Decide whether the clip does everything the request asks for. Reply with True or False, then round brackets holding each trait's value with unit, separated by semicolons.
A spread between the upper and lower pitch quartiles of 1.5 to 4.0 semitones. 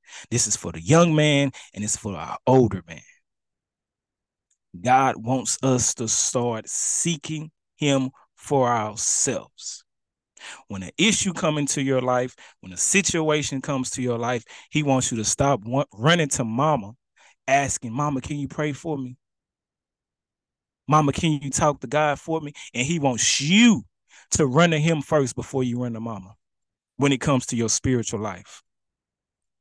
False (4.7 semitones)